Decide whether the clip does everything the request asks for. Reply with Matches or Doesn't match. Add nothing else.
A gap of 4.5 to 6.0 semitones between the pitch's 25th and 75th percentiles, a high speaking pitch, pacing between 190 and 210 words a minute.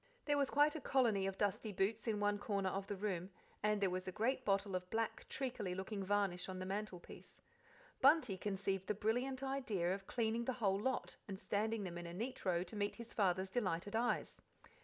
Doesn't match